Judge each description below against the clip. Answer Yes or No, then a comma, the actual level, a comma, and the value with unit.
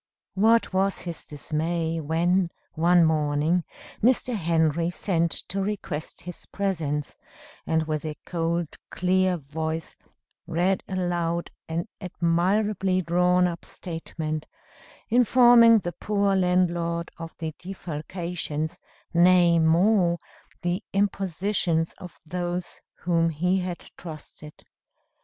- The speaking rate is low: Yes, slow, 105 wpm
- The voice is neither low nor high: Yes, medium, 175 Hz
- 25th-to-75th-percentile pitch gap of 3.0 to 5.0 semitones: No, narrow, 2.4 semitones